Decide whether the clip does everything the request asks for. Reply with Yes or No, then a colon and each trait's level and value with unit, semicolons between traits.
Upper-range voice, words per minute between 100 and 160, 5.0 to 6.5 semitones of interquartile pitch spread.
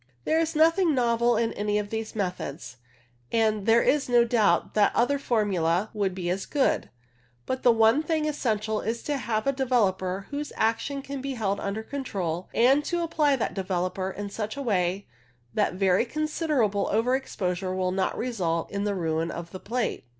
No: high, 220 Hz; average, 180 wpm; wide, 5.4 semitones